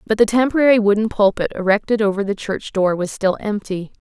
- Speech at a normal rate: Yes, average, 195 wpm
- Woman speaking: Yes, female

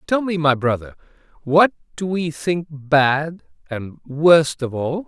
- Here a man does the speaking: Yes, male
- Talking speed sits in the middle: Yes, average, 155 wpm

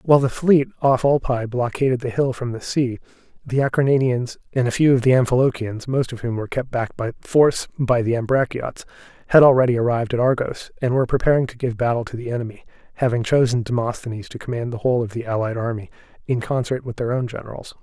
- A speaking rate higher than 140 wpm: Yes, fast, 205 wpm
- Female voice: No, male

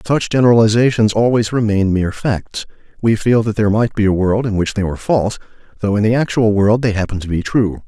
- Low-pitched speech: Yes, low, 110 Hz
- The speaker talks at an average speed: No, fast, 220 wpm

